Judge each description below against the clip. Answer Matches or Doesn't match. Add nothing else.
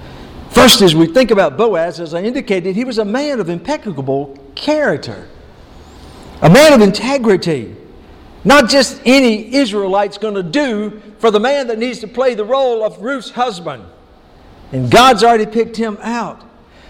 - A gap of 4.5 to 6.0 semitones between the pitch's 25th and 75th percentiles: Matches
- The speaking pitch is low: Doesn't match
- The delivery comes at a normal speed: Matches